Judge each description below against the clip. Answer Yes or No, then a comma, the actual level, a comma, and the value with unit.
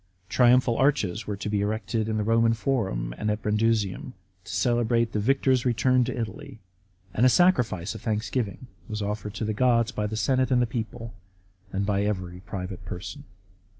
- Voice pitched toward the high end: No, low, 110 Hz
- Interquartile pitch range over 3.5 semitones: No, average, 2.9 semitones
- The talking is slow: No, average, 175 wpm